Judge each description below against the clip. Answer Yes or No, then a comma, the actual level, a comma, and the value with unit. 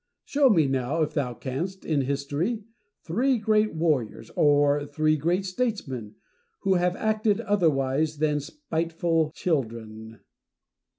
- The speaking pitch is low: No, medium, 155 Hz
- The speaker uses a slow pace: Yes, slow, 120 wpm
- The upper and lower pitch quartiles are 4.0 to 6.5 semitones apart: Yes, wide, 5.4 semitones